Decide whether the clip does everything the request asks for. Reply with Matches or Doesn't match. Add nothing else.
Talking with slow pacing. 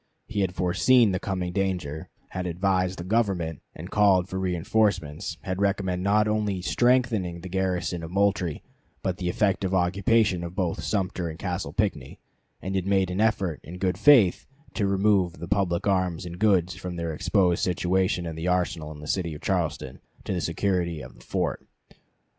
Doesn't match